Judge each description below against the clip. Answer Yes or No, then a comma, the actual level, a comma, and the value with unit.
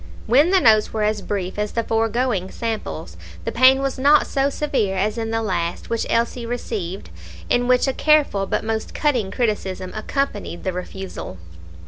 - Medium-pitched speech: No, high, 225 Hz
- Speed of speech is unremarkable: Yes, average, 170 wpm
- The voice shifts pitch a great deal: No, average, 4.5 semitones